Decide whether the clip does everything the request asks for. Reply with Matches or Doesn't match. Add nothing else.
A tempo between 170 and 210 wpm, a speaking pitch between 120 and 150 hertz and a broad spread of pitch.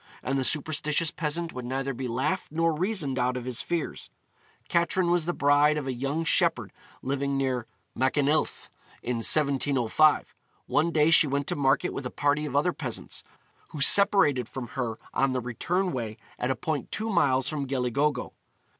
Doesn't match